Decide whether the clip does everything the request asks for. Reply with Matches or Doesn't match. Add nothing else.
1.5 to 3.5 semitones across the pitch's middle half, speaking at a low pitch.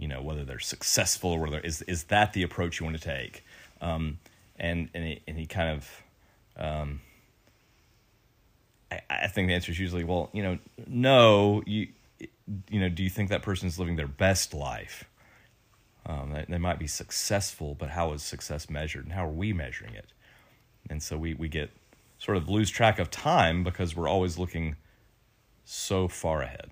Doesn't match